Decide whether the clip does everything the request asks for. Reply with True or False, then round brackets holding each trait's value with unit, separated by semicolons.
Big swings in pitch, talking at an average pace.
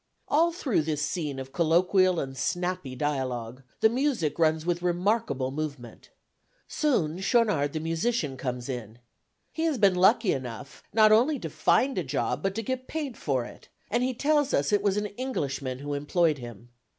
True (8.3 semitones; 175 wpm)